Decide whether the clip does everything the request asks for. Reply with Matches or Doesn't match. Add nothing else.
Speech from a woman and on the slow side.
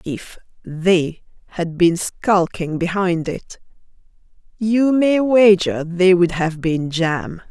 Matches